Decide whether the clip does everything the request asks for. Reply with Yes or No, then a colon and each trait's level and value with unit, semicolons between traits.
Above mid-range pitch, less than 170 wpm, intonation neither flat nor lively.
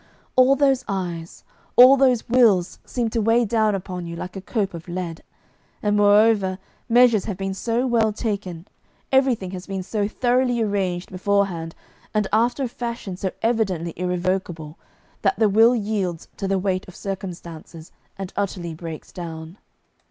Yes: high, 195 Hz; average, 155 wpm; average, 4.1 semitones